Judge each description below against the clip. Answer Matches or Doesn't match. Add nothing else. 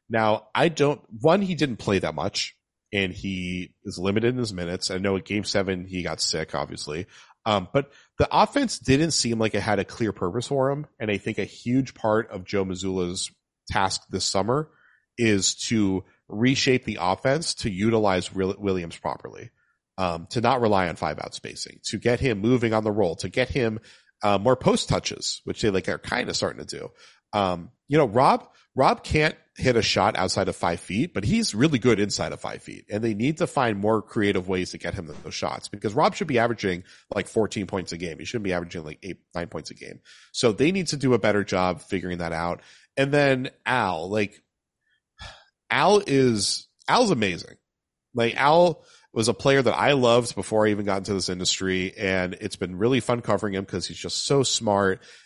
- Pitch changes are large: Doesn't match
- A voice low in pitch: Matches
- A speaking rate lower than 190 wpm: Doesn't match